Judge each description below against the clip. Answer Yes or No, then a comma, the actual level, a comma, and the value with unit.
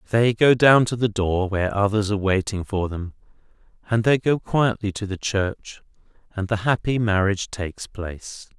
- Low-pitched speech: Yes, low, 105 Hz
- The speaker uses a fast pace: No, average, 175 wpm